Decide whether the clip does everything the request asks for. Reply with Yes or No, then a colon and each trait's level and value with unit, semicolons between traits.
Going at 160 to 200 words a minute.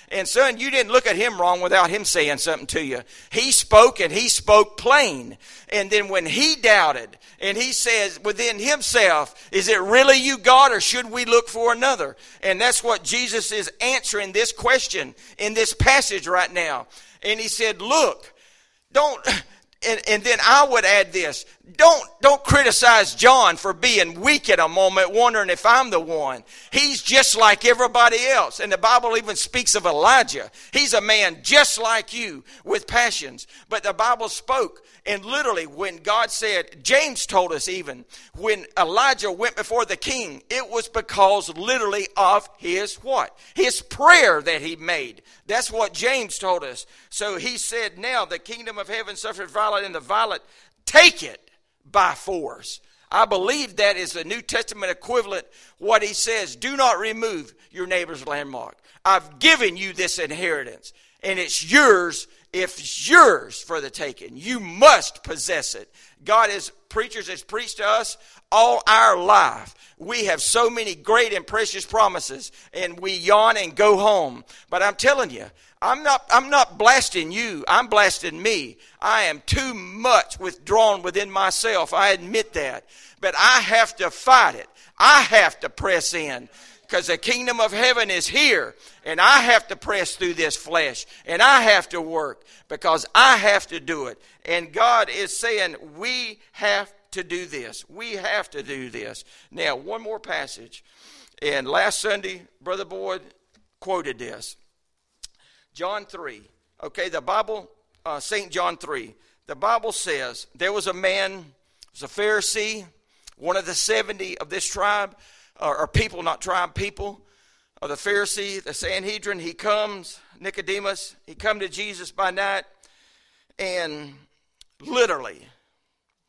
Yes: average, 165 wpm